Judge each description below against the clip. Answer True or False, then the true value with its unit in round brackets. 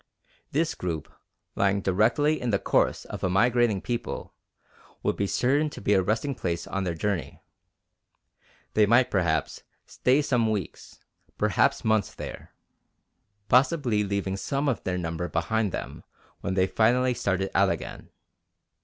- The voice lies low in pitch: True (105 Hz)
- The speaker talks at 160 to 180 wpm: False (145 wpm)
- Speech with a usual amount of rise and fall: True (4.6 semitones)